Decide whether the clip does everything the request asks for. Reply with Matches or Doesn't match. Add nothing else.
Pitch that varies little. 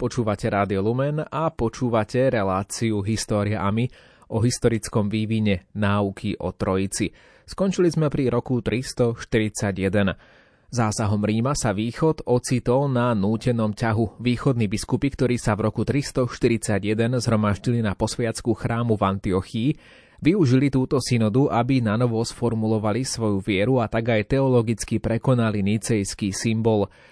Doesn't match